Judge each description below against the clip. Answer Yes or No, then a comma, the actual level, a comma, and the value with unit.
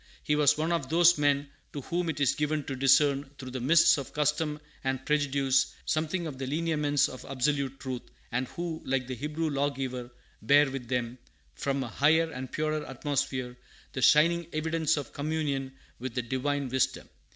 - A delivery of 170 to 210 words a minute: Yes, average, 175 wpm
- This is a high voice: No, medium, 145 Hz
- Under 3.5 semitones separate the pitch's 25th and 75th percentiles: Yes, average, 2.7 semitones